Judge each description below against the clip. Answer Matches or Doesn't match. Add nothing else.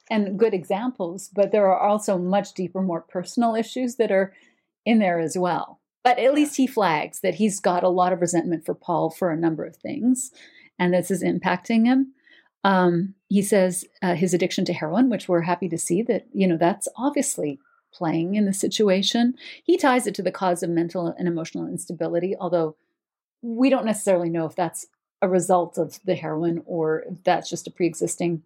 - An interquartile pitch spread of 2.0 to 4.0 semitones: Doesn't match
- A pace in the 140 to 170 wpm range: Doesn't match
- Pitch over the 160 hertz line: Matches